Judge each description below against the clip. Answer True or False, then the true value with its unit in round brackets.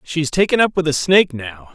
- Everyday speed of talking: False (275 wpm)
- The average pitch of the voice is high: False (155 Hz)